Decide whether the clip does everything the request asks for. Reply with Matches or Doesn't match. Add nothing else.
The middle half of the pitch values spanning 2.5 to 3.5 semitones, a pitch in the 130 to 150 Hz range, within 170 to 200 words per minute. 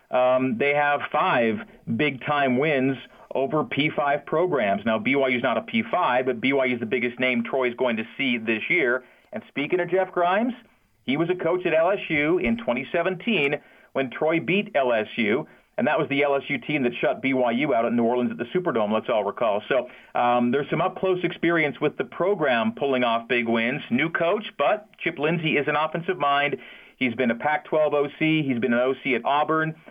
Doesn't match